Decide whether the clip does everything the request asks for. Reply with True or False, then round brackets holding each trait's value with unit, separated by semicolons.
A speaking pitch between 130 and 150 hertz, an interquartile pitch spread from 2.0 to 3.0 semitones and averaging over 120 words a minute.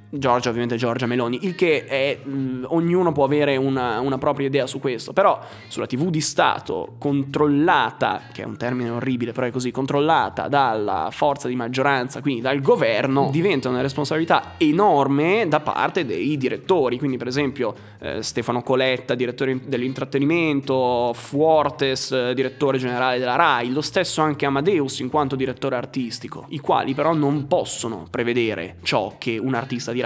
True (135 Hz; 2.6 semitones; 160 wpm)